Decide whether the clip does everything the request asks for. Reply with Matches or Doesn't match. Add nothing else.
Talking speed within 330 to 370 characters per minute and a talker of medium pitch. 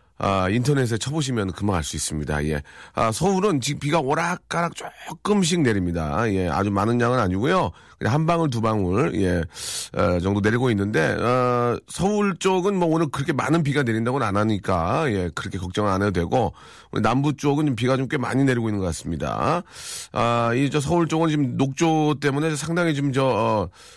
Doesn't match